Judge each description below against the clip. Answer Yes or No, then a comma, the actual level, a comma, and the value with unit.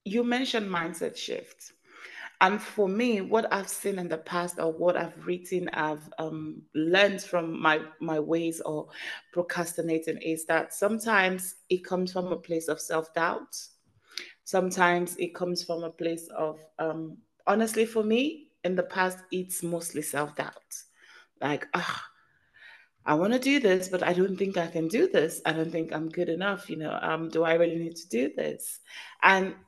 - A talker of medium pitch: Yes, medium, 175 Hz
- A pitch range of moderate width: Yes, average, 3.1 semitones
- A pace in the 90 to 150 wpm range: No, average, 170 wpm